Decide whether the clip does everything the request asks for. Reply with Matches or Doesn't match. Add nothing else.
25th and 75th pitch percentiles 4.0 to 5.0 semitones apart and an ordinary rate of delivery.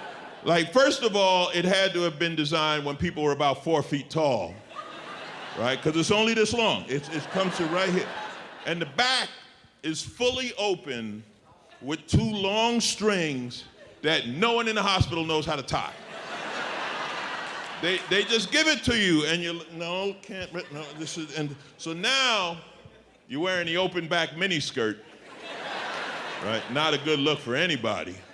Matches